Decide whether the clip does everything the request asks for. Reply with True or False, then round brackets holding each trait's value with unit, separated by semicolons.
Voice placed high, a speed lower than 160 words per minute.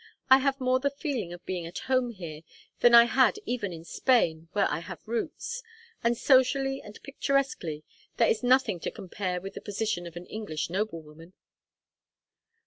False (215 Hz; 170 wpm)